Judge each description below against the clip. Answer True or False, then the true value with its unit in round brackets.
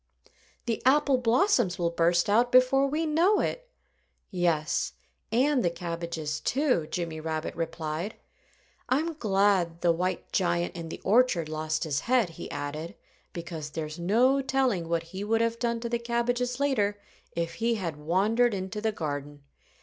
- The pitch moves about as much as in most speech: False (6.6 semitones)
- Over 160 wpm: False (155 wpm)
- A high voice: True (195 Hz)